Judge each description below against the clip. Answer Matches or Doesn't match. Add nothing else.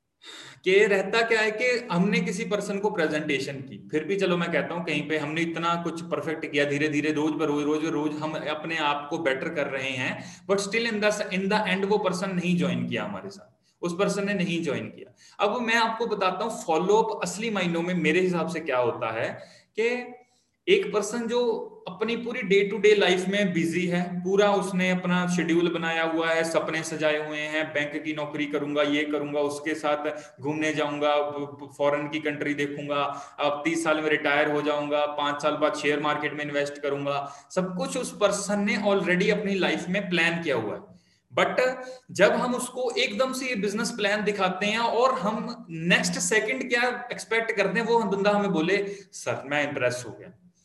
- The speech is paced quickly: Matches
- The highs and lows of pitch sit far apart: Matches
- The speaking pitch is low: Doesn't match